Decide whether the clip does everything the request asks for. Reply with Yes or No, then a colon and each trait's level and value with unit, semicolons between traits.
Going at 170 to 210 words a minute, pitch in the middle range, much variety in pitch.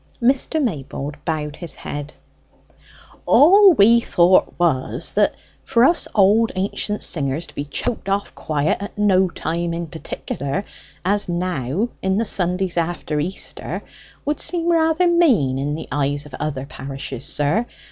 No: average, 145 wpm; medium, 175 Hz; wide, 7.3 semitones